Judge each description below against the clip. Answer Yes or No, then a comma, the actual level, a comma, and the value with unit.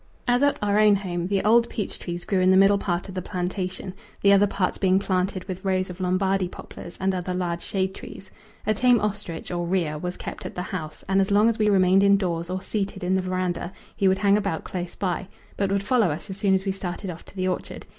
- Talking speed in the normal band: No, fast, 245 wpm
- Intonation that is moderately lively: No, narrow, 1.7 semitones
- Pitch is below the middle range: No, high, 190 Hz